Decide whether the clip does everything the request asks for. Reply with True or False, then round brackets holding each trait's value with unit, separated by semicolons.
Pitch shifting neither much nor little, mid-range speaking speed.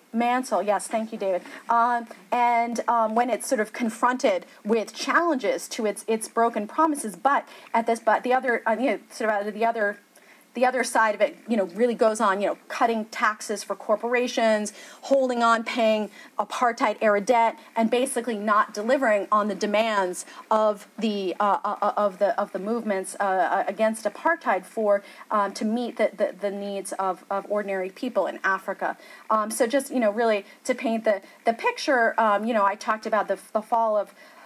True (3.0 semitones; 190 wpm)